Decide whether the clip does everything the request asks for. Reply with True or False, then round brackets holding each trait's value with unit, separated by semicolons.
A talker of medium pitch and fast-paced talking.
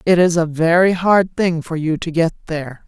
True (165 Hz; 230 wpm)